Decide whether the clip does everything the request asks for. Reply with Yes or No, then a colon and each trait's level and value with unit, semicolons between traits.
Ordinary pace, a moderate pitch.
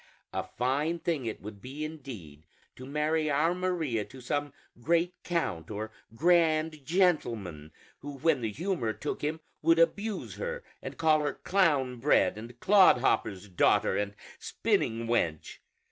Yes: average, 145 wpm; medium, 145 Hz